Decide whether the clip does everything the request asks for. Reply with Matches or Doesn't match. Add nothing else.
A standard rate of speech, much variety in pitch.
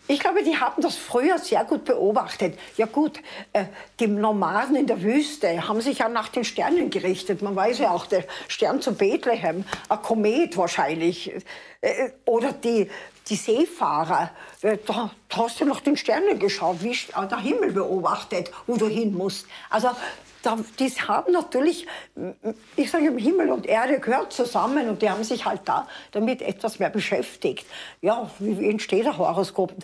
Matches